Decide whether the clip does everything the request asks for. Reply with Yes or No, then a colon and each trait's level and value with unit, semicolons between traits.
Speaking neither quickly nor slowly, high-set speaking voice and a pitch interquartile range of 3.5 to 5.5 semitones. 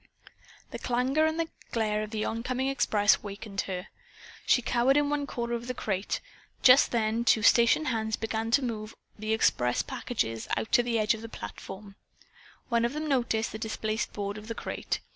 No: average, 180 wpm; high, 225 Hz; average, 2.7 semitones